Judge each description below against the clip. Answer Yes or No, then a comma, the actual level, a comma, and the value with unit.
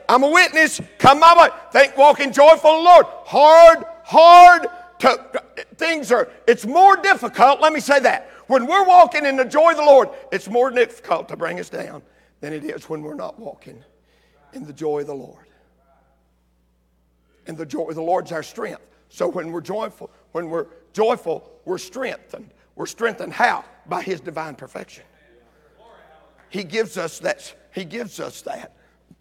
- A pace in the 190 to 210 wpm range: No, average, 175 wpm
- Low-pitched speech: No, high, 245 Hz